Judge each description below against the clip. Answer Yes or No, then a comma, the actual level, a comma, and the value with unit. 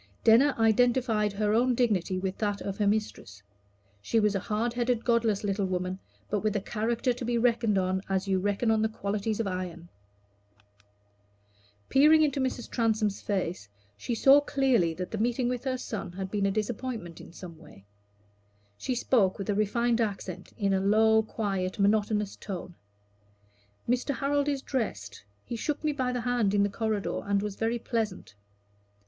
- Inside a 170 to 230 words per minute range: Yes, average, 175 wpm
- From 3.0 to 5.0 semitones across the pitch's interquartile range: Yes, average, 3.6 semitones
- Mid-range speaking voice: No, high, 215 Hz